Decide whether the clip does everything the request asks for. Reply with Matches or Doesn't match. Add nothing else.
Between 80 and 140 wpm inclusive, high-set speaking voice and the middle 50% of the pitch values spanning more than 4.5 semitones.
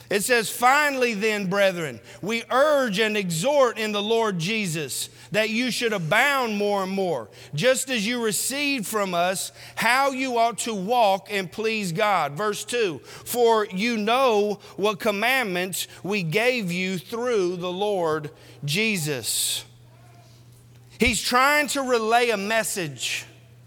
Matches